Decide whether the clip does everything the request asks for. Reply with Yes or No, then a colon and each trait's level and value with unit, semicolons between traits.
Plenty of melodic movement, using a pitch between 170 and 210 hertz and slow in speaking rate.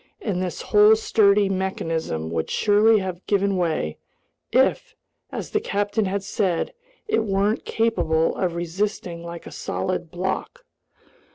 No: average, 3.3 semitones; high, 190 Hz; slow, 130 wpm